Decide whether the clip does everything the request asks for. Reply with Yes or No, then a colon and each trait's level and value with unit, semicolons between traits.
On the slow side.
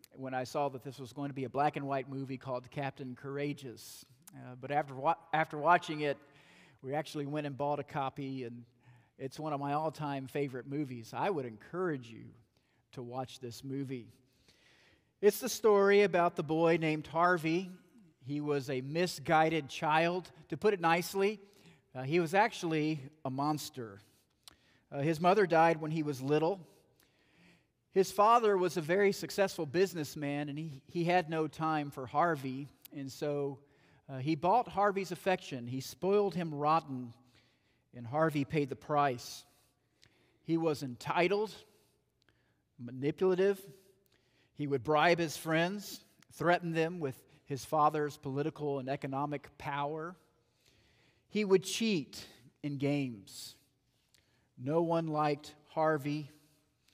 No: average, 145 wpm